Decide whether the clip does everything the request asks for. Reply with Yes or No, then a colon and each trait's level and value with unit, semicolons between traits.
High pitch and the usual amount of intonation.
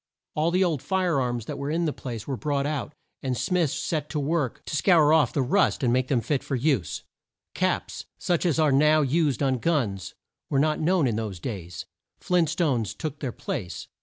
No: medium, 145 Hz; average, 4.3 semitones